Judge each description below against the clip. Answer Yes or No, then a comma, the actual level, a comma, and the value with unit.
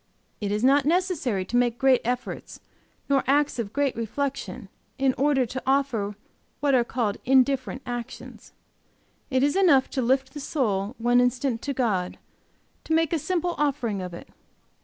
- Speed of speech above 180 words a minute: No, average, 160 wpm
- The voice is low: No, very high, 260 Hz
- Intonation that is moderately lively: Yes, average, 3.2 semitones